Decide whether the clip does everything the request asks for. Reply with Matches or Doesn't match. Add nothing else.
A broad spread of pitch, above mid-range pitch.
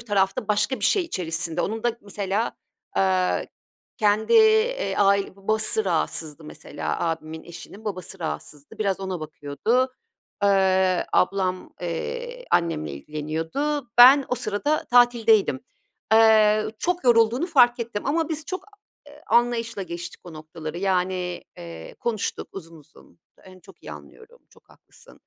Matches